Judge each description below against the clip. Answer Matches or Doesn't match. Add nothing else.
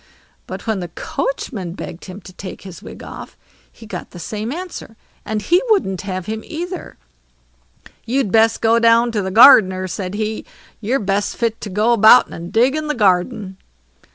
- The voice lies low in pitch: Doesn't match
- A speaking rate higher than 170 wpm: Matches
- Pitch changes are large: Doesn't match